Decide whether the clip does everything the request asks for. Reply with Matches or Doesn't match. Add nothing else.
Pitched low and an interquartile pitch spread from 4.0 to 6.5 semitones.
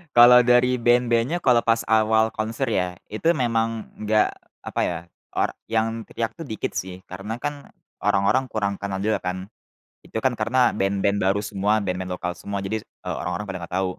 Doesn't match